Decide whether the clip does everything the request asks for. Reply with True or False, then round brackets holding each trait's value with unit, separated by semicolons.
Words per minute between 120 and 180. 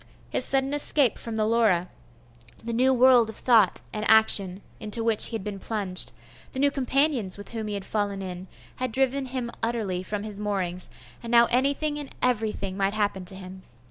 False (190 wpm)